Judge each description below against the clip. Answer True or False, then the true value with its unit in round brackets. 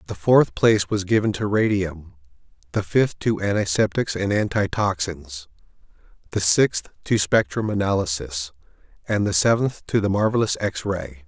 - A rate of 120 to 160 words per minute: True (140 wpm)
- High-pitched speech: False (105 Hz)